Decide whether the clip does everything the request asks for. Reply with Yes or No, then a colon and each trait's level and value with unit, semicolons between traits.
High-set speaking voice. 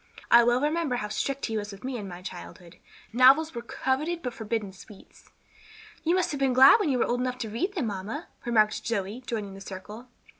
Yes: high, 240 Hz